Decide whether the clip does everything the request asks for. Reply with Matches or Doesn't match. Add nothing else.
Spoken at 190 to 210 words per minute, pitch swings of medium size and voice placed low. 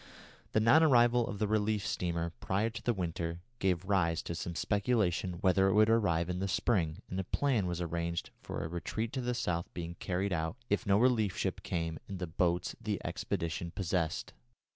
Matches